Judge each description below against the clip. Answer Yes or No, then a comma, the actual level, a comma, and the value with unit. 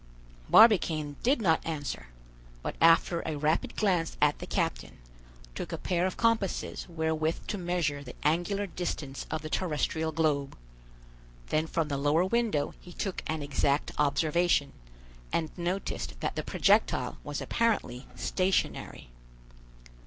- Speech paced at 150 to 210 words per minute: No, slow, 135 wpm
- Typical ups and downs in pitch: Yes, average, 3.6 semitones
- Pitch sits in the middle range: Yes, medium, 160 Hz